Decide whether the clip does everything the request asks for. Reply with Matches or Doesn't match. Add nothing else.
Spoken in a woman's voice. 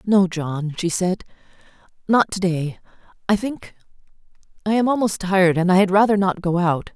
Matches